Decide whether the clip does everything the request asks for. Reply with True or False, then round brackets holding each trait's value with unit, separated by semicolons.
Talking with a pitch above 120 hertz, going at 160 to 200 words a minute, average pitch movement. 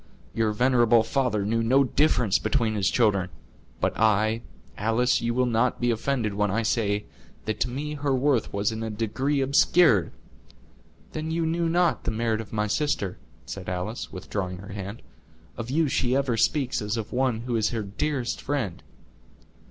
False (115 Hz; 170 wpm; 3.9 semitones)